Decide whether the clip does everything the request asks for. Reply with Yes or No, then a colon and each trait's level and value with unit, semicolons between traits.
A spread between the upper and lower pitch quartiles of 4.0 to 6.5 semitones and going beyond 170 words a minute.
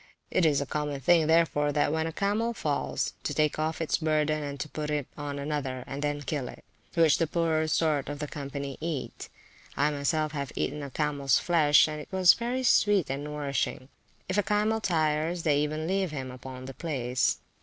No: narrow, 2.4 semitones; average, 195 wpm